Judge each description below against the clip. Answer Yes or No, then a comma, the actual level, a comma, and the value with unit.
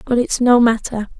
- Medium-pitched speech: No, high, 235 Hz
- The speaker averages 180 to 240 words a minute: Yes, average, 200 wpm